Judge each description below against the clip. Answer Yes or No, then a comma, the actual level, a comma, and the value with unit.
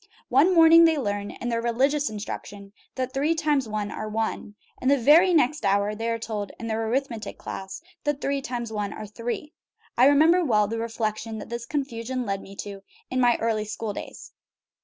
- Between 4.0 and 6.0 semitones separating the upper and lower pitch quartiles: Yes, average, 4.6 semitones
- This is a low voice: No, high, 230 Hz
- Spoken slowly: No, average, 195 wpm